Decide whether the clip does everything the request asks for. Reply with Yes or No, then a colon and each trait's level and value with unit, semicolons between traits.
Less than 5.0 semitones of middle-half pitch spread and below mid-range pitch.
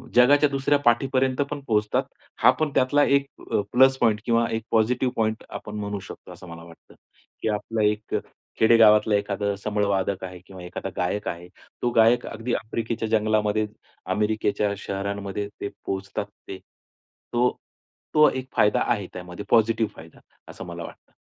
Yes: average, 2.8 semitones; low, 110 Hz